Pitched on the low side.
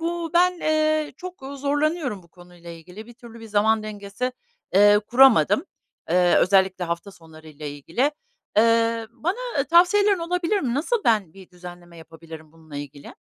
No: high, 215 Hz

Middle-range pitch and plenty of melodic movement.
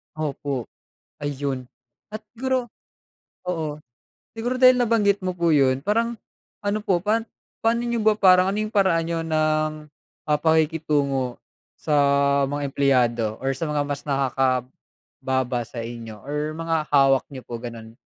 Yes: medium, 150 Hz; wide, 6.5 semitones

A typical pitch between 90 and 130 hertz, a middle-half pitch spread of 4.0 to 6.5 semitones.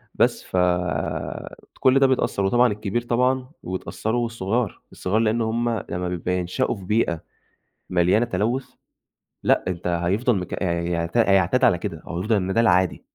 Yes: low, 100 Hz; average, 4.7 semitones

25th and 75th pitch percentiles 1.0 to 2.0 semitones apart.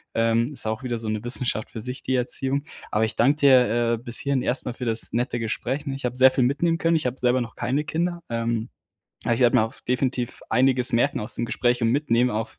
No: narrow, 2.4 semitones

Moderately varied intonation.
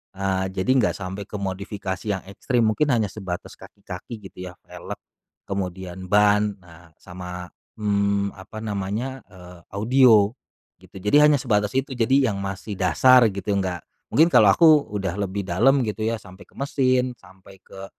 Yes: average, 3.4 semitones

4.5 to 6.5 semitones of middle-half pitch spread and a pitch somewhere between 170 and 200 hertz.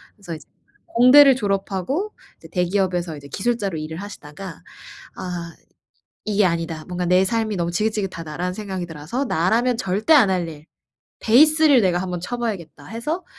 Yes: average, 5.1 semitones; high, 190 Hz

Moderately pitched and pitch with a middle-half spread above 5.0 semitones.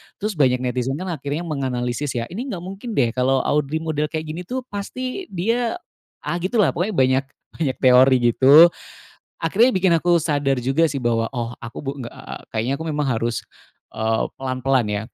Yes: medium, 145 Hz; wide, 5.4 semitones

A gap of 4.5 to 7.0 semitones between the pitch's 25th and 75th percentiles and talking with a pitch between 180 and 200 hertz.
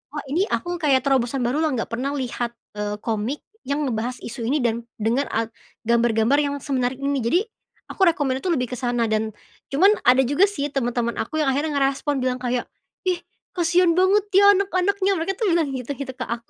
No: average, 4.9 semitones; very high, 270 Hz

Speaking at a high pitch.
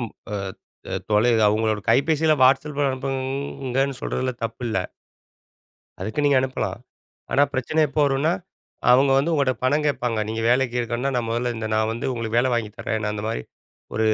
No: low, 125 Hz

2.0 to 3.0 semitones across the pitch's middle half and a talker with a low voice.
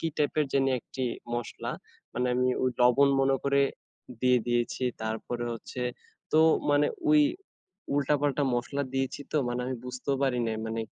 Yes: narrow, 2.5 semitones; low, 130 Hz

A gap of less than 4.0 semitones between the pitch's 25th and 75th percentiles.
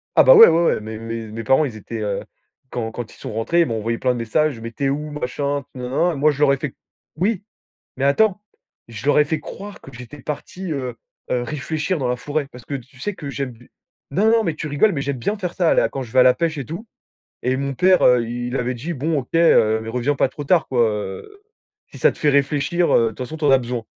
No: average, 4.5 semitones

